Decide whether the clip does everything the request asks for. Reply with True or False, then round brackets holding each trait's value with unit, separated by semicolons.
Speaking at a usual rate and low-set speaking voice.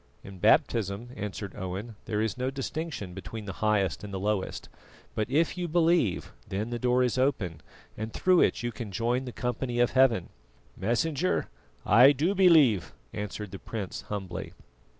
True (165 wpm; 115 Hz)